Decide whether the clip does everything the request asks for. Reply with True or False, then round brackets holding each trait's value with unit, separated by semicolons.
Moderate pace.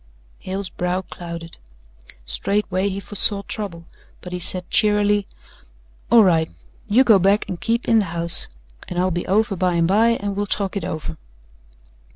True (165 wpm)